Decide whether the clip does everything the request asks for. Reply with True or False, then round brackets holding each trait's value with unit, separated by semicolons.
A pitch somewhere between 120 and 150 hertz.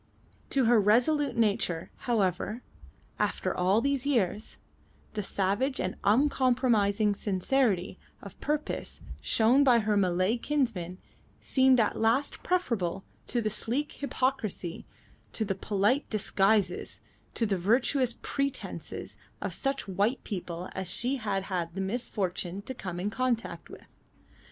False (220 Hz)